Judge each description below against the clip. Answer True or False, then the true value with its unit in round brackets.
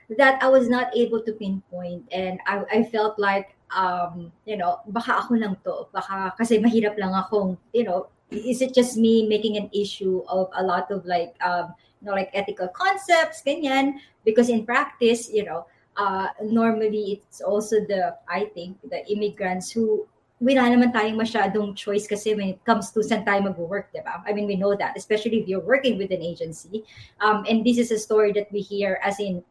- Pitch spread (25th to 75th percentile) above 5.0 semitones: False (3.1 semitones)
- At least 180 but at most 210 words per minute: True (195 wpm)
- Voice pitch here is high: True (210 Hz)